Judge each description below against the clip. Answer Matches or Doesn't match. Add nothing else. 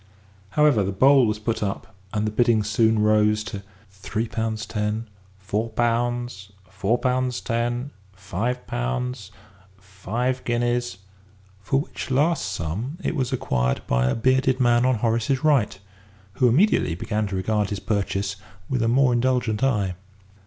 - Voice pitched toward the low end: Matches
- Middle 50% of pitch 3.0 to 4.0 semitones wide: Matches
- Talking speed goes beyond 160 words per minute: Doesn't match